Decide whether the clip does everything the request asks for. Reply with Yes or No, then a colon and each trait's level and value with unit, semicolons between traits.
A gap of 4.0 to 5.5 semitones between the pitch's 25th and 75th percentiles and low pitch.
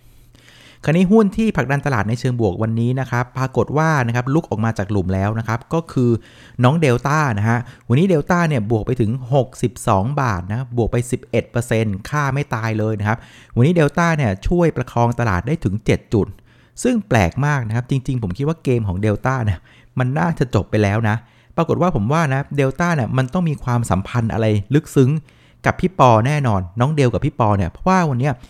Yes: average, 4.5 semitones; low, 125 Hz